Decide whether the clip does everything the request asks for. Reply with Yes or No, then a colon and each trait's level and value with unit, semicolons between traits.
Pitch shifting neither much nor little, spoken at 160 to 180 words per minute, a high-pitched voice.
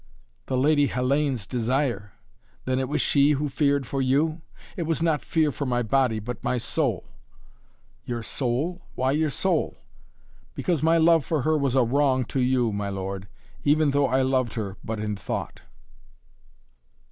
No: average, 3.6 semitones; average, 165 wpm; low, 135 Hz